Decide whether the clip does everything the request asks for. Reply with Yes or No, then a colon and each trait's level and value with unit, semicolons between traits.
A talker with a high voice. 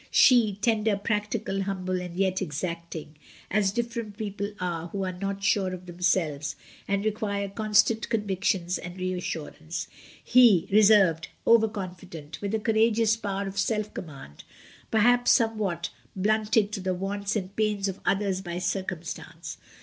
Yes: high, 195 Hz